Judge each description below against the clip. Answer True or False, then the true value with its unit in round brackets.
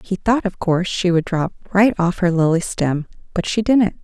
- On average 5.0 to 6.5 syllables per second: False (4.6 syllables/s)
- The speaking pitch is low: False (185 Hz)